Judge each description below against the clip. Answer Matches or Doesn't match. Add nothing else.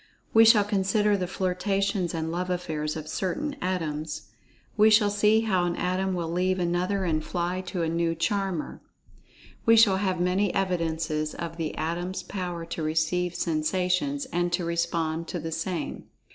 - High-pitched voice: Doesn't match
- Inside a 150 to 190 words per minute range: Matches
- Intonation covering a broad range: Doesn't match